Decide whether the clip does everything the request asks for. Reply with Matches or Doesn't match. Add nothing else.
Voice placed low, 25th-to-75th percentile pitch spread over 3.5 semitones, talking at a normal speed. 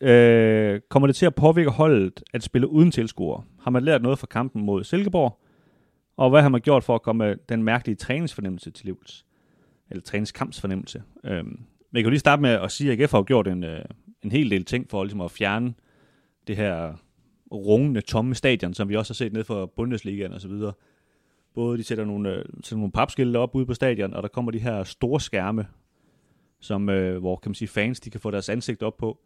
Matches